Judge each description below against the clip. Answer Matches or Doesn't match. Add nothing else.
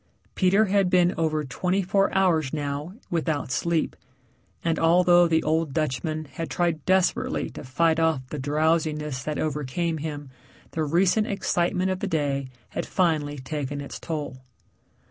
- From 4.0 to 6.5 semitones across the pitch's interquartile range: Doesn't match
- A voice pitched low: Doesn't match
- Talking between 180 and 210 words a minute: Doesn't match